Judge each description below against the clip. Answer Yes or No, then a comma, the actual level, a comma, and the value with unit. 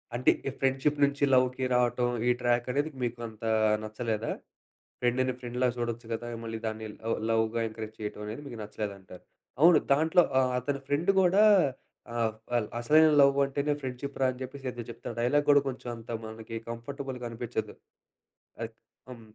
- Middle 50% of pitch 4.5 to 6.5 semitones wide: No, average, 3.4 semitones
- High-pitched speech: No, low, 120 Hz